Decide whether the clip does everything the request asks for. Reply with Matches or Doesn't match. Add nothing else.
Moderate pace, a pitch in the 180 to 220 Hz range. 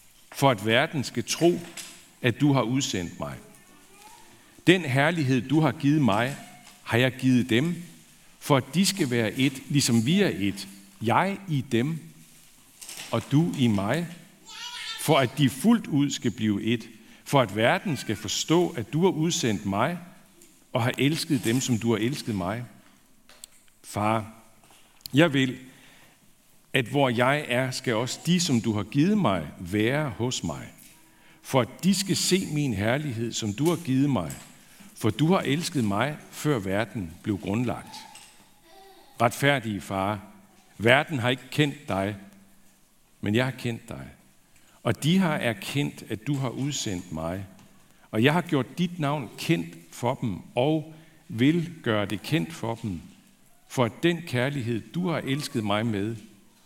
Doesn't match